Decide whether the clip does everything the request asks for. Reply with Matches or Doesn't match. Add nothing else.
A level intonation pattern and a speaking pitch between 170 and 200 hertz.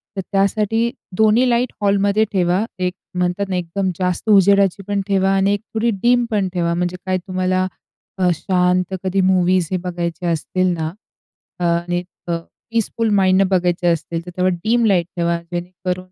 Matches